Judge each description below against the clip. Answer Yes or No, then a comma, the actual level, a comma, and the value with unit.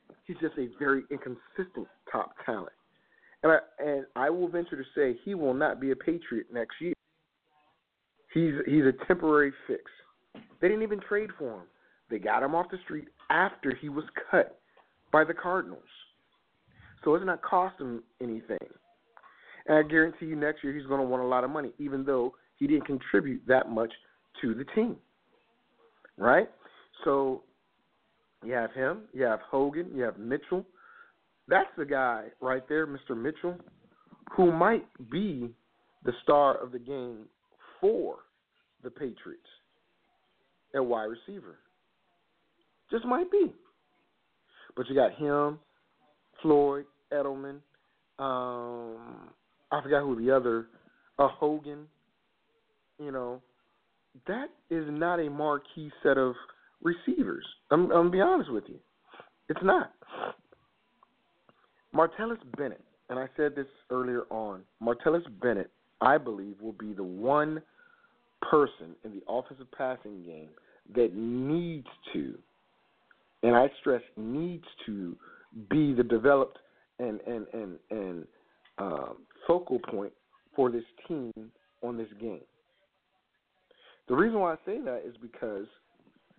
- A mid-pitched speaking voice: Yes, medium, 145 Hz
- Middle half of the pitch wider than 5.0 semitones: Yes, wide, 5.4 semitones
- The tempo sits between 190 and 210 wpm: No, average, 140 wpm